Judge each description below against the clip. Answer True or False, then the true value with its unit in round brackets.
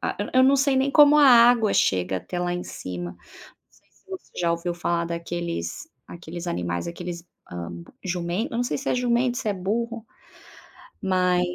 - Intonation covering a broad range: True (6.1 semitones)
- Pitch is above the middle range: False (180 Hz)